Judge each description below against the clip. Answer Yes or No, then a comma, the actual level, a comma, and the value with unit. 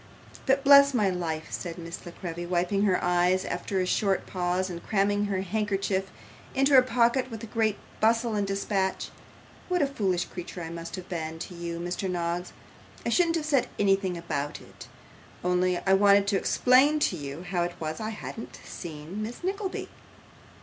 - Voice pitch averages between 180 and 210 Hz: Yes, high, 190 Hz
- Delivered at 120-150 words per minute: No, average, 175 wpm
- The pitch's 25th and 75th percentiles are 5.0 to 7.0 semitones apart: No, average, 4.2 semitones